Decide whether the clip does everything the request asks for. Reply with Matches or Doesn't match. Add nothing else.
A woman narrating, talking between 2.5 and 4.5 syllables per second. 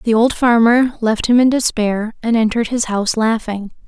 Doesn't match